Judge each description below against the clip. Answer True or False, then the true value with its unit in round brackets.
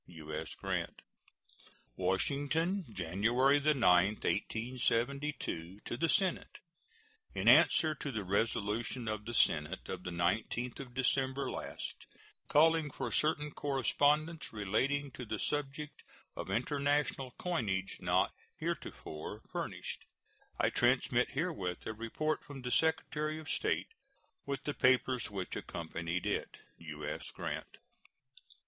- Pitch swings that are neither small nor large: False (6.5 semitones)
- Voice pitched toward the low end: True (125 Hz)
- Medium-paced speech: False (115 wpm)